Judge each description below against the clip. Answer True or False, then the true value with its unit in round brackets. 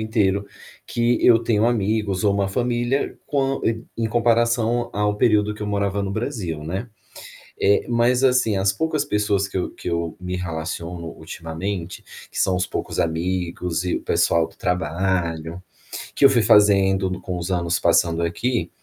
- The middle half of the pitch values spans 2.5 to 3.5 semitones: False (4.6 semitones)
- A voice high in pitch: False (100 Hz)